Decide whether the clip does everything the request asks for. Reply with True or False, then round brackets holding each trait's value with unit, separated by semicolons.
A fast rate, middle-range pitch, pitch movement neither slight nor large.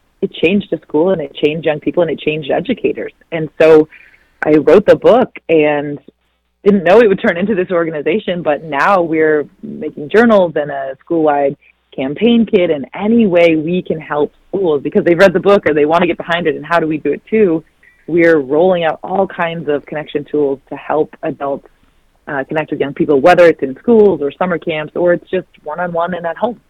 True (210 wpm; 165 Hz; 3.6 semitones)